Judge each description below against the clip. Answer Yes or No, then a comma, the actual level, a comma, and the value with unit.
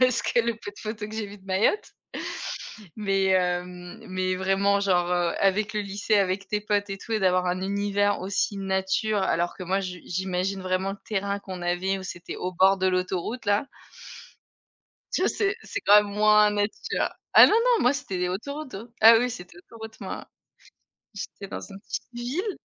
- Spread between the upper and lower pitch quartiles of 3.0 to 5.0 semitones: No, narrow, 2.4 semitones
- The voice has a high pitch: Yes, high, 200 Hz